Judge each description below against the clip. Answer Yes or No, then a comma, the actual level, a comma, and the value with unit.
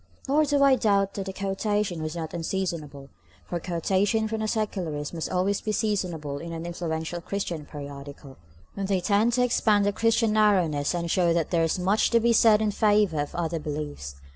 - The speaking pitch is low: No, medium, 185 Hz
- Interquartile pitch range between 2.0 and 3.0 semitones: No, average, 4.7 semitones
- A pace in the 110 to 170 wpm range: No, average, 190 wpm